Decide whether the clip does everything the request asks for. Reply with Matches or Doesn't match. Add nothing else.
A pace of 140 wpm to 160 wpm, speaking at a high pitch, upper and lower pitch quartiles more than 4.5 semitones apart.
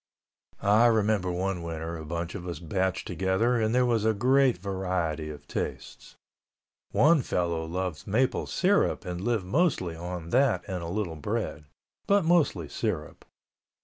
Doesn't match